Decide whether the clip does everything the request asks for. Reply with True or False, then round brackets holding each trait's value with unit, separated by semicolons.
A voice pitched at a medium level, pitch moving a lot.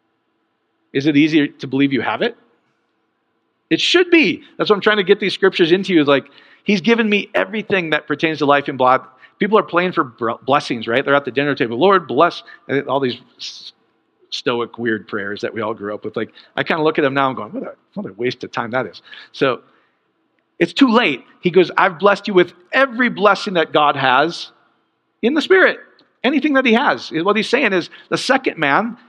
True (180 Hz; 7.9 semitones)